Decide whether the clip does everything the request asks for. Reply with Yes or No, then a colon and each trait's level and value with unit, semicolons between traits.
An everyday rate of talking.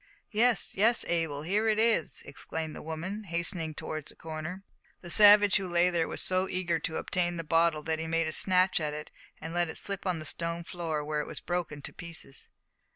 No: fast, 215 wpm